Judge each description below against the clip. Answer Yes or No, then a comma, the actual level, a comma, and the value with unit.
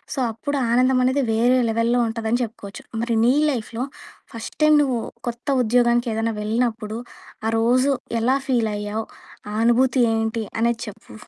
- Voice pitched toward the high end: Yes, high, 235 Hz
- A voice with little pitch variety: Yes, narrow, 2.0 semitones